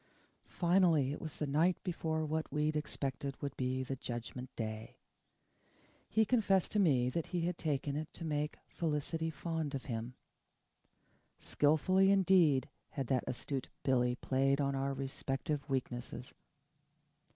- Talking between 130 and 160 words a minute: Yes, average, 140 wpm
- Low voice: No, medium, 145 Hz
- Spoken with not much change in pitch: No, average, 3.7 semitones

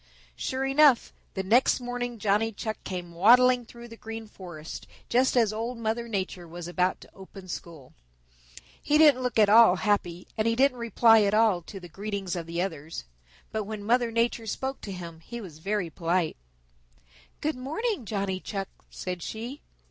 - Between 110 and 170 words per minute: No, average, 180 wpm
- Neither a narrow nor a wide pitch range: Yes, average, 4.6 semitones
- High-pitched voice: Yes, high, 215 Hz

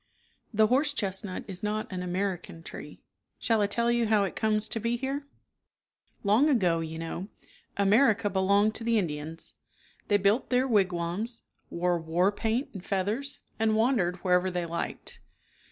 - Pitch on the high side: Yes, high, 205 Hz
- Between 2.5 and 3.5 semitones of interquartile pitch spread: No, average, 4.1 semitones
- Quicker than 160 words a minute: No, average, 155 wpm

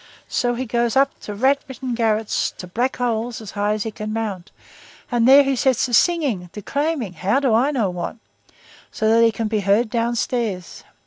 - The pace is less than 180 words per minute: No, average, 195 wpm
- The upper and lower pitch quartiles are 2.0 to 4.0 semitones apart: Yes, average, 3.4 semitones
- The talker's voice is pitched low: No, high, 230 Hz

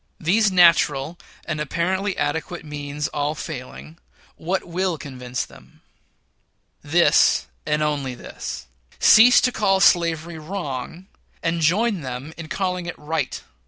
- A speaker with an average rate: No, slow, 125 wpm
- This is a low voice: No, medium, 160 Hz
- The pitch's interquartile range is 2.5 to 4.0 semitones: Yes, average, 3.7 semitones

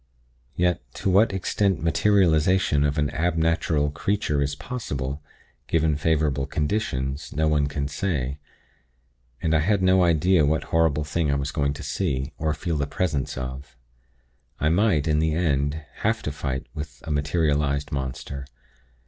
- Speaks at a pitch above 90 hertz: No, very low, 75 Hz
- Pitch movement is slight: No, average, 3.0 semitones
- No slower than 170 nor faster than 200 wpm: No, average, 155 wpm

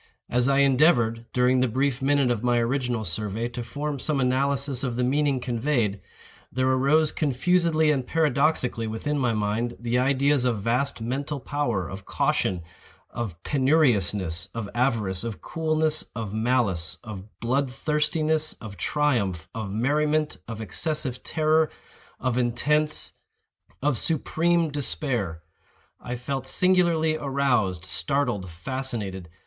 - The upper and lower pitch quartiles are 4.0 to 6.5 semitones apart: Yes, average, 4.5 semitones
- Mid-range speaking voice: No, low, 130 Hz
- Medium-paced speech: No, slow, 130 wpm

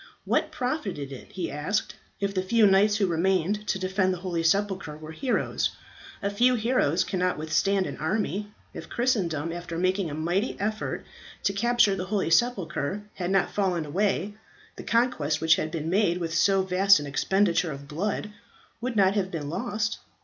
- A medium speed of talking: Yes, average, 175 wpm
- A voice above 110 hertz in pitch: Yes, high, 190 Hz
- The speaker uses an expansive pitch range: No, average, 3.8 semitones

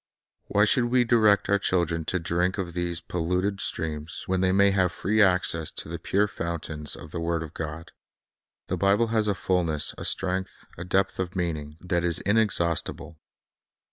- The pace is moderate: Yes, average, 180 wpm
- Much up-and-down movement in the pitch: No, average, 3.1 semitones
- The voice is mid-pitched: No, very low, 90 Hz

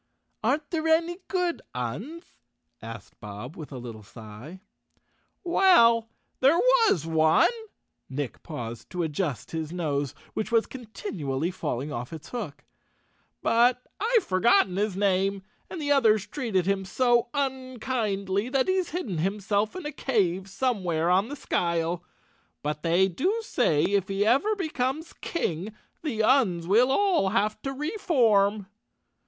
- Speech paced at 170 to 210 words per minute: No, average, 145 wpm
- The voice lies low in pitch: No, high, 205 Hz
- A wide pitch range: Yes, wide, 8.1 semitones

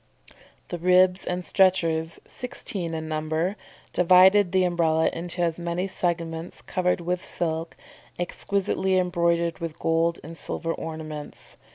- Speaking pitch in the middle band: Yes, medium, 170 Hz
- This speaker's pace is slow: Yes, slow, 125 wpm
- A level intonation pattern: Yes, narrow, 1.9 semitones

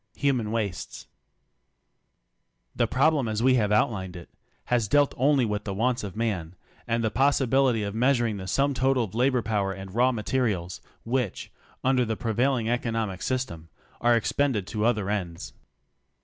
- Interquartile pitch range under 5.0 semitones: Yes, average, 3.8 semitones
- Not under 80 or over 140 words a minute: No, average, 160 wpm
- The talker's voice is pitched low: Yes, low, 115 Hz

